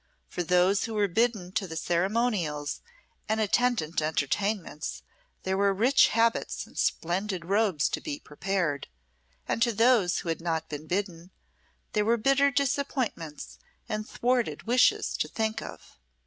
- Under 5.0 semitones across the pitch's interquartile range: No, average, 5.3 semitones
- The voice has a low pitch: No, high, 200 Hz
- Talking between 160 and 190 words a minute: No, average, 145 wpm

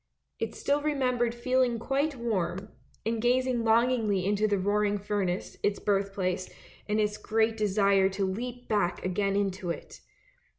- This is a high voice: Yes, high, 210 Hz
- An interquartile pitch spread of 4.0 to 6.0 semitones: No, average, 3.4 semitones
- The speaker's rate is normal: Yes, average, 145 wpm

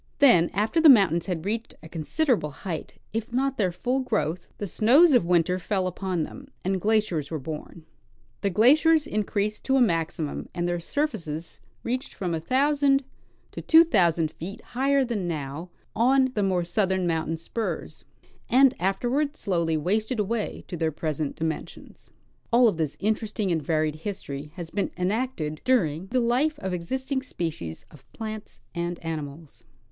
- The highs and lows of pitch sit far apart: Yes, wide, 7.0 semitones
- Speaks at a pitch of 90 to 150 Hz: No, high, 190 Hz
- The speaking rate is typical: Yes, average, 160 wpm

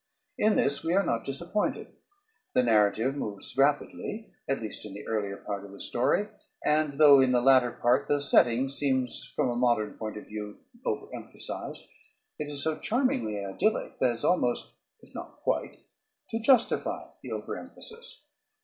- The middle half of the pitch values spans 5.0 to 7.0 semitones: Yes, wide, 5.5 semitones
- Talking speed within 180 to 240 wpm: No, average, 165 wpm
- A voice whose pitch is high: No, low, 130 Hz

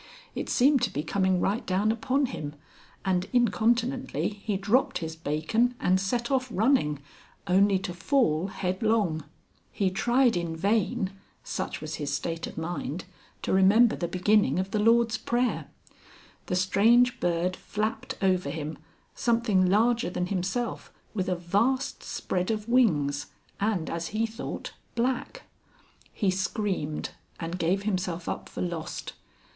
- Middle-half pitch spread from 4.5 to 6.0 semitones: Yes, average, 4.8 semitones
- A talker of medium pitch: No, high, 195 Hz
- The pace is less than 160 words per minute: Yes, average, 140 wpm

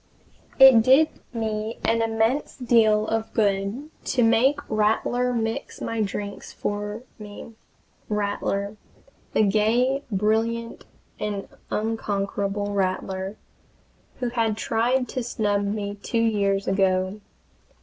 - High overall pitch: Yes, high, 215 Hz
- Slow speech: Yes, slow, 110 wpm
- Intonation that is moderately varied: No, narrow, 2.2 semitones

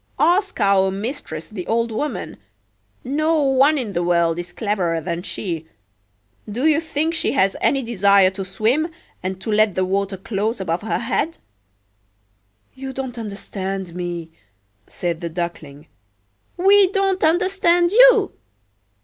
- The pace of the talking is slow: Yes, slow, 130 wpm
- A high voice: Yes, high, 200 Hz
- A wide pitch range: Yes, wide, 8.5 semitones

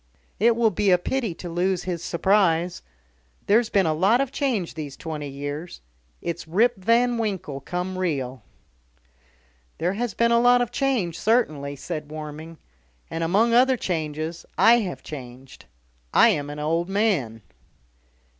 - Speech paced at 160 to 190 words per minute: No, average, 150 wpm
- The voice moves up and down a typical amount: No, wide, 6.5 semitones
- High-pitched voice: No, medium, 180 Hz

